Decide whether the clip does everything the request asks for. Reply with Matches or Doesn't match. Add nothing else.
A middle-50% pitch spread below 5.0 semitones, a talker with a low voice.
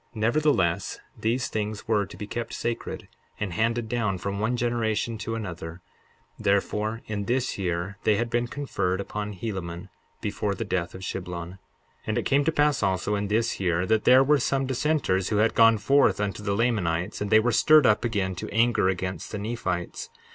Matches